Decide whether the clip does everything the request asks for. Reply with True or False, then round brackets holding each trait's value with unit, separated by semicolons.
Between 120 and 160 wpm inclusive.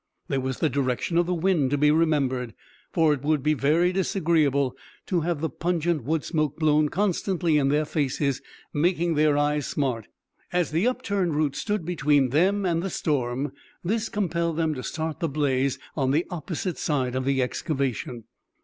False (175 wpm)